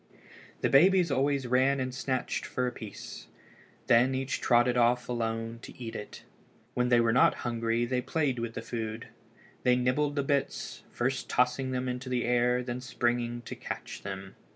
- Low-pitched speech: Yes, low, 125 Hz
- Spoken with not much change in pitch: Yes, narrow, 1.7 semitones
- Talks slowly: No, average, 175 wpm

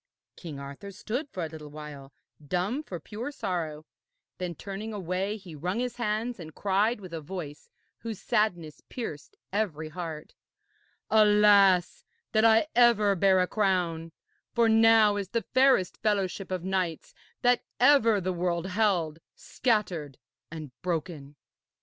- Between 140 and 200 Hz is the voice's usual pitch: Yes, high, 190 Hz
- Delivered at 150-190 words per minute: No, average, 140 wpm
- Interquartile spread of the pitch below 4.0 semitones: No, average, 4.7 semitones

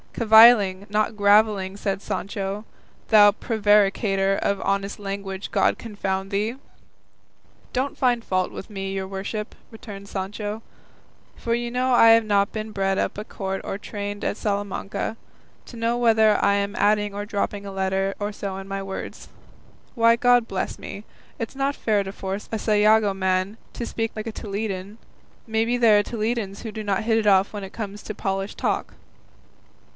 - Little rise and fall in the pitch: Yes, narrow, 2.1 semitones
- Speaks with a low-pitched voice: No, high, 205 Hz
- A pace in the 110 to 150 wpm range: No, average, 170 wpm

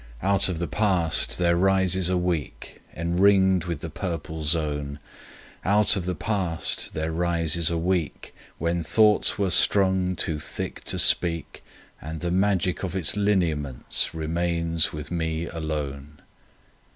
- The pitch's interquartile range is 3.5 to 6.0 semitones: No, average, 2.7 semitones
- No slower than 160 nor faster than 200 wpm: No, average, 140 wpm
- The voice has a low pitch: Yes, very low, 85 Hz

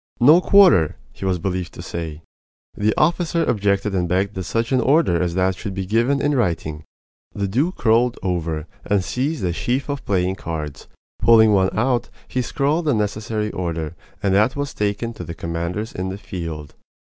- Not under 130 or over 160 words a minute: No, average, 180 wpm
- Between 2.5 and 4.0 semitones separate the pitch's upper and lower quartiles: No, wide, 5.6 semitones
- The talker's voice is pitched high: No, low, 100 Hz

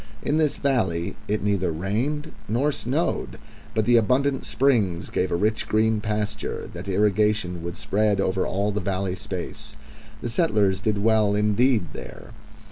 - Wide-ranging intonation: No, average, 3.5 semitones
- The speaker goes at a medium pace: Yes, average, 150 wpm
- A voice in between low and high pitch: No, low, 105 Hz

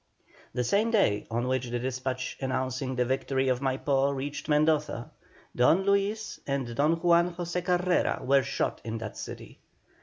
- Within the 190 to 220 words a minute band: No, average, 155 wpm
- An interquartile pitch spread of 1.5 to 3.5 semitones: No, average, 4.9 semitones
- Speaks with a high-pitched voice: No, low, 135 Hz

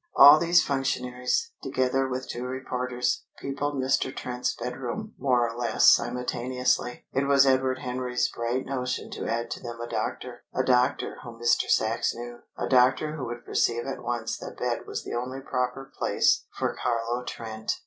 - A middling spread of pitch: No, narrow, 1.7 semitones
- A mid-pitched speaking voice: No, low, 125 Hz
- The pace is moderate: Yes, average, 170 wpm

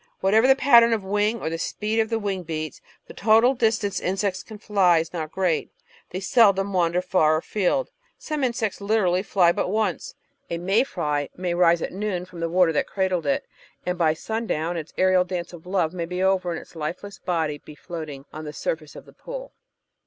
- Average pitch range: Yes, average, 3.9 semitones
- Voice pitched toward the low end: No, medium, 185 Hz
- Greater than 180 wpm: Yes, fast, 205 wpm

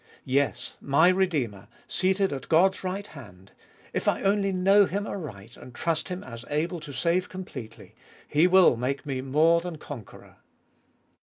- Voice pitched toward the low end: No, medium, 160 Hz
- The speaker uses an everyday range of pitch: No, wide, 5.8 semitones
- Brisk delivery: No, average, 165 wpm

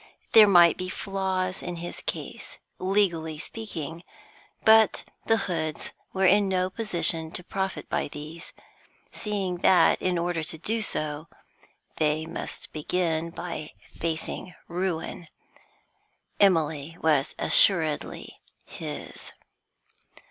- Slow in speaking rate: Yes, slow, 110 wpm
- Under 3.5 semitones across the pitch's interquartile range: Yes, average, 3.0 semitones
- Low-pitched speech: No, medium, 175 Hz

